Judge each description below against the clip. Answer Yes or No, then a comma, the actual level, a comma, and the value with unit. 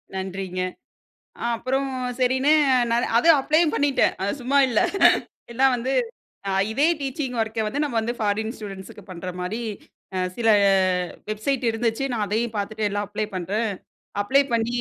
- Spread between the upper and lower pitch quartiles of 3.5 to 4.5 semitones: Yes, average, 4.2 semitones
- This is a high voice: Yes, high, 225 Hz